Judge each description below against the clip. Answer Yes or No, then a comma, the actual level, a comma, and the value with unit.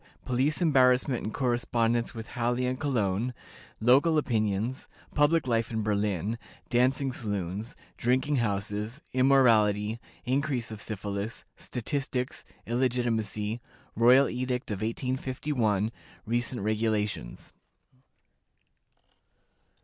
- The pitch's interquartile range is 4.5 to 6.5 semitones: No, average, 3.1 semitones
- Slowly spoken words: Yes, slow, 90 wpm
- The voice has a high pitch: No, low, 120 Hz